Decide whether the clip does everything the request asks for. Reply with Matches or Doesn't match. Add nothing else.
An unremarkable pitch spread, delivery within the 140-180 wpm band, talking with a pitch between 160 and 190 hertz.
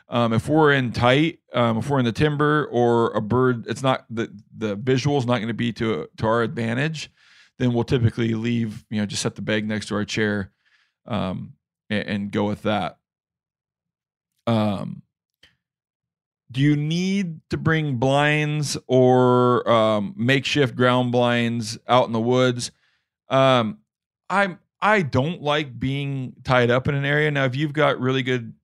Doesn't match